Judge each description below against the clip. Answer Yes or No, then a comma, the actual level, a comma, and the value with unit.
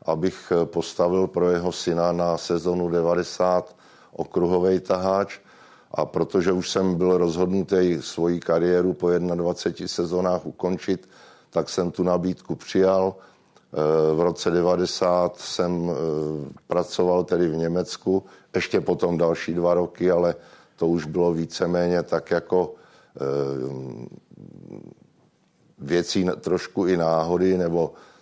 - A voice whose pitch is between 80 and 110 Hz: Yes, very low, 90 Hz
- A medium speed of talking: No, slow, 110 wpm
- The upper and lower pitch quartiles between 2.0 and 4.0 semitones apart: No, narrow, 1.3 semitones